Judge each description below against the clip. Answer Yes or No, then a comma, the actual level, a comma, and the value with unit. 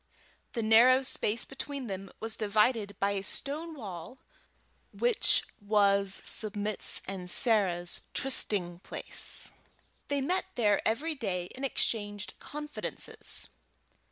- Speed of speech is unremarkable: No, slow, 110 wpm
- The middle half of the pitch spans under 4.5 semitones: No, average, 4.9 semitones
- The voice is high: Yes, high, 215 Hz